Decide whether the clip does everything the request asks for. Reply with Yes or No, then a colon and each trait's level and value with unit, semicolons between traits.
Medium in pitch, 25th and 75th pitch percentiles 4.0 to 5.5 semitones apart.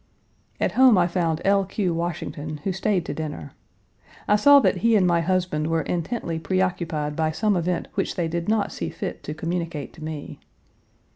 No: medium, 170 Hz; average, 3.2 semitones